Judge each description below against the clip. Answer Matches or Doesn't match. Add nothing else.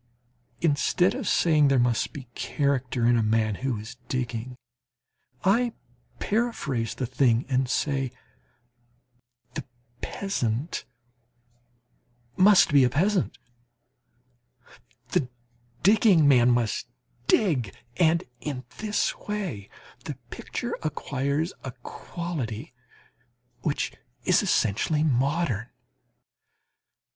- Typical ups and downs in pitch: Doesn't match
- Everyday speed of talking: Doesn't match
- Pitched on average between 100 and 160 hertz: Matches